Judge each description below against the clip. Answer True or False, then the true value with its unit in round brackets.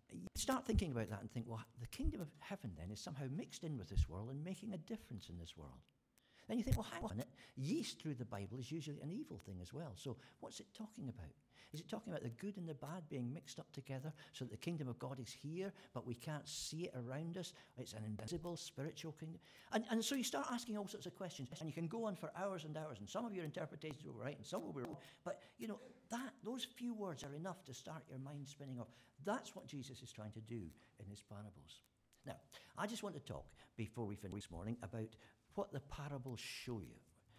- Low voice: False (145 Hz)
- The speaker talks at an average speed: False (250 wpm)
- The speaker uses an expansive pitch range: True (7.8 semitones)